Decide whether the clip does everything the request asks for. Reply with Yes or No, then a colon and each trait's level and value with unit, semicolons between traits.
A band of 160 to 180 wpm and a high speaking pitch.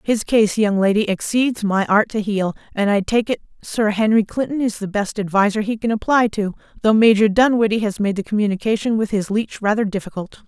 No: fast, 205 wpm; high, 210 Hz